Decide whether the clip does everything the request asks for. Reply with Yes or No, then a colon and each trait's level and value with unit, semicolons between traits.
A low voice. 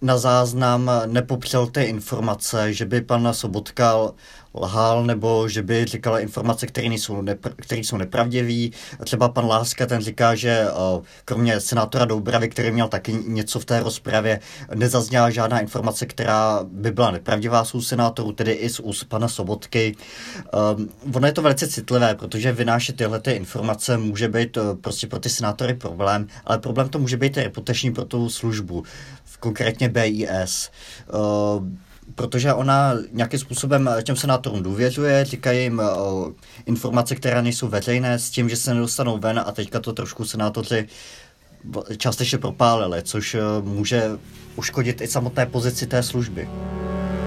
Yes: low, 115 Hz